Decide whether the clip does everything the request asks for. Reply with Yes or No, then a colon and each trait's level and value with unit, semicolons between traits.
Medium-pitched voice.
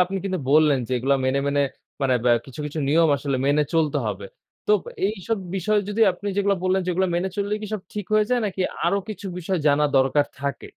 Yes: medium, 170 Hz